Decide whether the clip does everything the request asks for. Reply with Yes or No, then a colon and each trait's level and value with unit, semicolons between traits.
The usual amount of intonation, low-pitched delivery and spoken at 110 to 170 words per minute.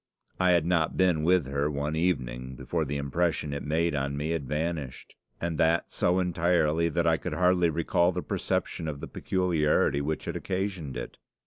No: average, 3.3 semitones; very low, 80 Hz; average, 185 wpm